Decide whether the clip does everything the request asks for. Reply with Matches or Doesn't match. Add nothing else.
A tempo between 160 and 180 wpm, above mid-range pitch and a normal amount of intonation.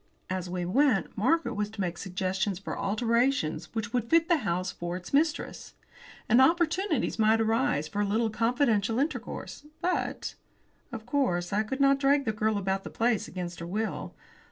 Doesn't match